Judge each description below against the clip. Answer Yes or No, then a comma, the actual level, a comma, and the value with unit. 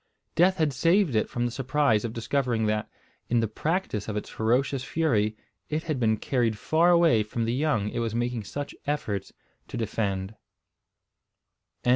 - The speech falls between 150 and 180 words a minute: Yes, average, 165 wpm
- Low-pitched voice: Yes, low, 120 Hz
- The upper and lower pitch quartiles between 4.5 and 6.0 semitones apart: Yes, average, 5.2 semitones